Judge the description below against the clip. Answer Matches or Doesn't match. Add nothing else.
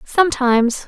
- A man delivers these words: Doesn't match